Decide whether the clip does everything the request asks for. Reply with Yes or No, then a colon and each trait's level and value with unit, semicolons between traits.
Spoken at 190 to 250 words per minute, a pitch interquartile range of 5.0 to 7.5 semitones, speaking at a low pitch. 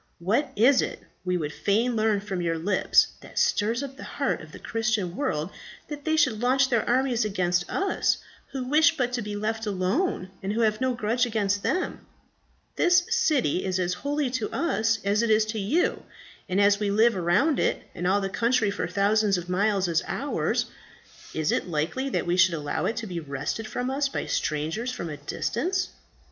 No: average, 200 wpm; wide, 5.4 semitones; high, 215 Hz